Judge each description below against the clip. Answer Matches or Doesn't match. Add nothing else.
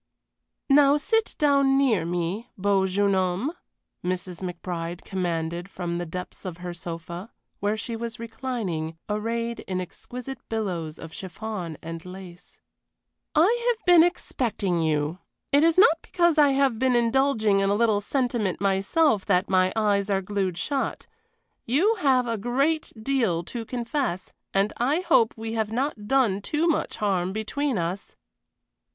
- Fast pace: Doesn't match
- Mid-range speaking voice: Doesn't match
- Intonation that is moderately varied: Doesn't match